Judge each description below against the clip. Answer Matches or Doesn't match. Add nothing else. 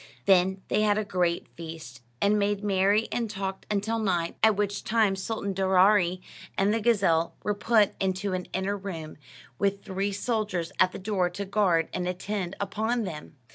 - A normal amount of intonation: Doesn't match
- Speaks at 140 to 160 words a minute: Doesn't match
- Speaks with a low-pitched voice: Doesn't match